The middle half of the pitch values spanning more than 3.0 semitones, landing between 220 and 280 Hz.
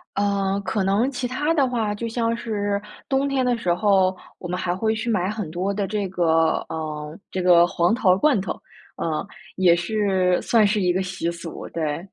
No: average, 3.9 semitones; high, 195 Hz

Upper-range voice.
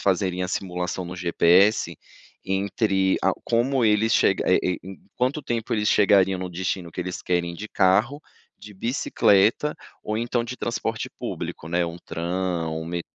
No: very low, 95 Hz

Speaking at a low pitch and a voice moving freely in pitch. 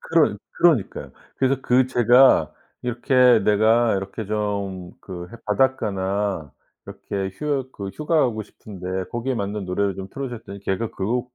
No: low, 105 Hz; average, 4.4 semitones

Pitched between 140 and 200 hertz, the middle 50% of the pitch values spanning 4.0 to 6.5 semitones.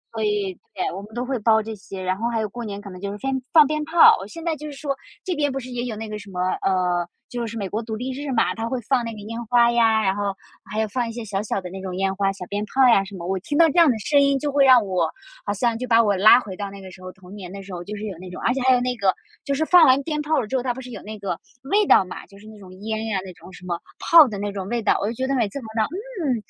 No: high, 220 Hz; average, 4.8 semitones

